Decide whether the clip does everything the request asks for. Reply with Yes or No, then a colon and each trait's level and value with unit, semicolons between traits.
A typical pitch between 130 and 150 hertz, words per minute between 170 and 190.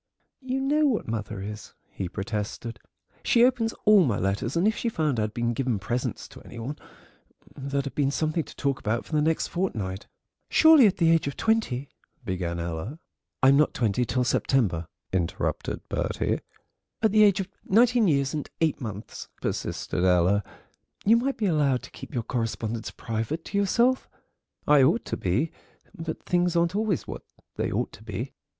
Yes: medium, 140 Hz; average, 175 wpm